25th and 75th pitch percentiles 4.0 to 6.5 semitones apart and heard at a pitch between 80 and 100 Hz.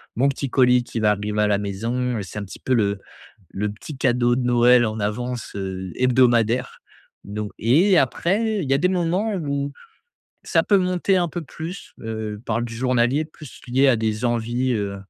No: average, 4.7 semitones; low, 125 Hz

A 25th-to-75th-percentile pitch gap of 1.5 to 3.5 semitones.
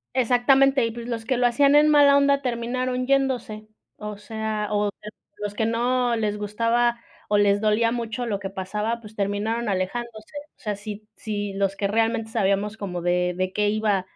Yes: average, 2.8 semitones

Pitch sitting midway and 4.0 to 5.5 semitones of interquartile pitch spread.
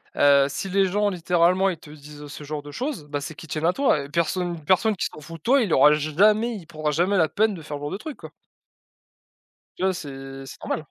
Yes: medium, 165 Hz; average, 4.7 semitones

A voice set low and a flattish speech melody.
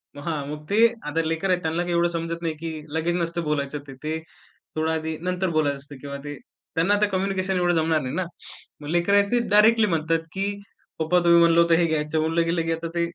No: medium, 165 Hz; narrow, 2.1 semitones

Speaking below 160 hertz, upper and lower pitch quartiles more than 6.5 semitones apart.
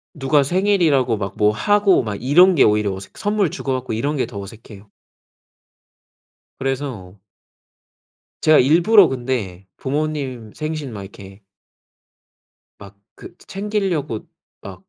Yes: low, 135 Hz; wide, 7.2 semitones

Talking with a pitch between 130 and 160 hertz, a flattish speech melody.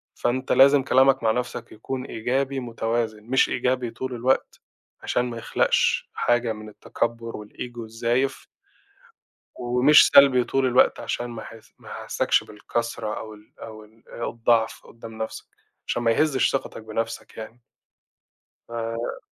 No: low, 120 Hz; narrow, 2.2 semitones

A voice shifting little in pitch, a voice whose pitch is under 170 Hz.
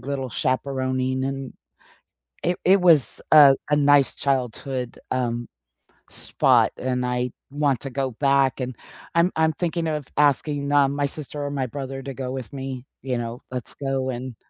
Yes: narrow, 1.9 semitones; low, 135 Hz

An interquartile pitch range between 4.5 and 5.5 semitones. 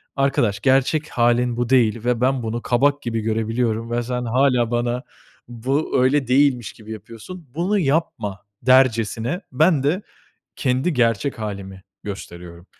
No: average, 3.3 semitones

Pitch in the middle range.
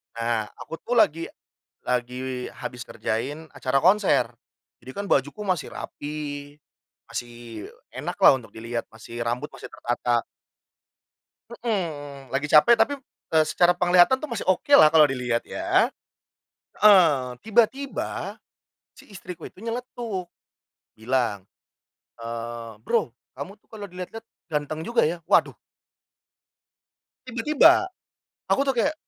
Yes: medium, 155 Hz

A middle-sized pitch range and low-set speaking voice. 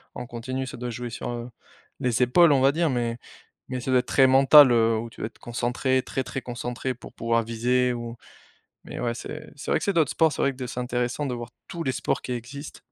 No: narrow, 2.0 semitones; low, 125 Hz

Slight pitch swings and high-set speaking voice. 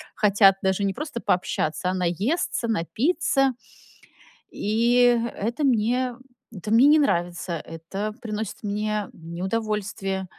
No: average, 4.0 semitones; high, 210 Hz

